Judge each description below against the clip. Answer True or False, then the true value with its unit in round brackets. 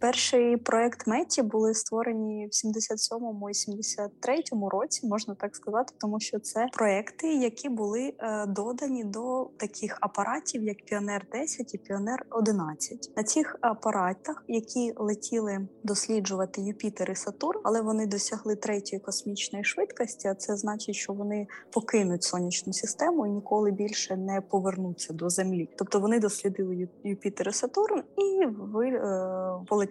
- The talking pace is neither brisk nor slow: True (140 wpm)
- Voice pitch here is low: False (215 Hz)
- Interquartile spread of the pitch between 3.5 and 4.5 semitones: False (2.7 semitones)